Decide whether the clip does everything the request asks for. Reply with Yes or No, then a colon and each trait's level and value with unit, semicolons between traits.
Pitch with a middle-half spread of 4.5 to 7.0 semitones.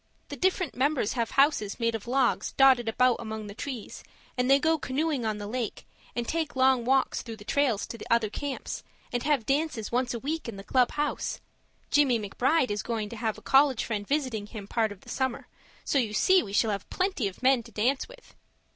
No: average, 4.1 semitones